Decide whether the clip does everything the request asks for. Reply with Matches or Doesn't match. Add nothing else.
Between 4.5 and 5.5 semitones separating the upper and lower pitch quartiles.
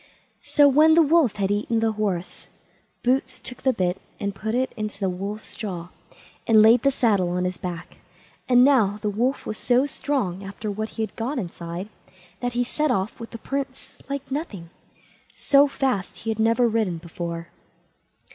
Matches